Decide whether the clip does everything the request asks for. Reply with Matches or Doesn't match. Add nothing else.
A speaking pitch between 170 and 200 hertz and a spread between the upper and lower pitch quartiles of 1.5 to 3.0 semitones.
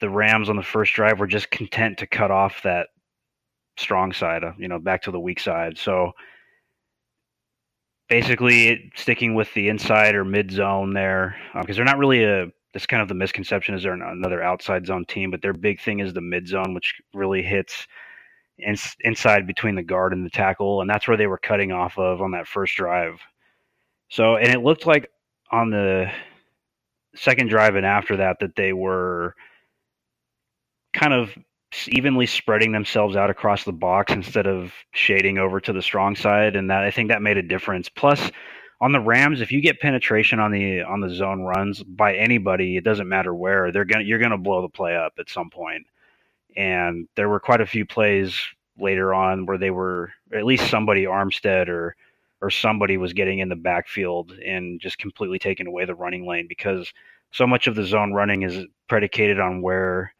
Doesn't match